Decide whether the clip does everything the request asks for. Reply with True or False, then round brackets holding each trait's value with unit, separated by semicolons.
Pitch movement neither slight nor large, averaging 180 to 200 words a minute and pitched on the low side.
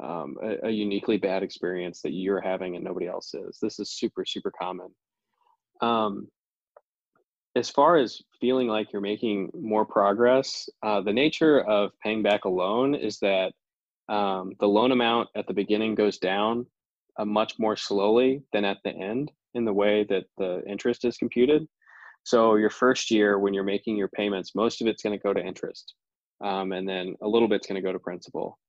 True (3.2 semitones; 185 wpm; 105 Hz)